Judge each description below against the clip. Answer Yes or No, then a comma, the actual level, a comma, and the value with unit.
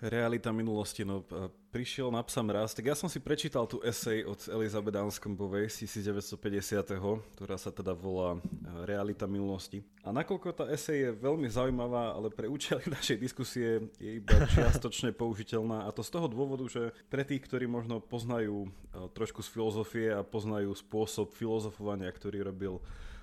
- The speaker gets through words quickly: No, average, 155 wpm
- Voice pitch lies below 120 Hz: Yes, low, 110 Hz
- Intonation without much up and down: No, average, 3.0 semitones